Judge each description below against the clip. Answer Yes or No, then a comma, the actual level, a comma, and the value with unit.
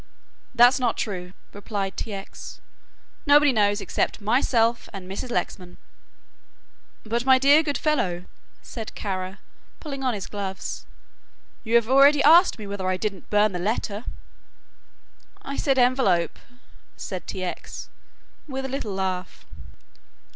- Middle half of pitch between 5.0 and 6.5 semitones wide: Yes, wide, 5.4 semitones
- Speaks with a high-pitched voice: Yes, high, 215 Hz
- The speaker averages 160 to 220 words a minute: No, slow, 135 wpm